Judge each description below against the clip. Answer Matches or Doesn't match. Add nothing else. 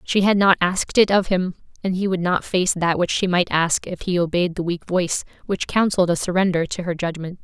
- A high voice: Doesn't match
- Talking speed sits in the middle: Doesn't match